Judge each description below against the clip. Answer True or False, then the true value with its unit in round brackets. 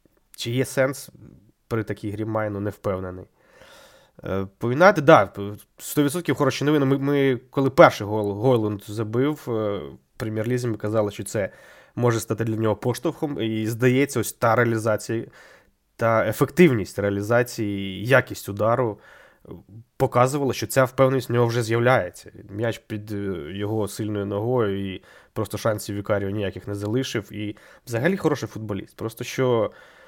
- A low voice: True (115 Hz)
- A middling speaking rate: True (135 wpm)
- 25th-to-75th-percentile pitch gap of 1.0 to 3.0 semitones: False (3.7 semitones)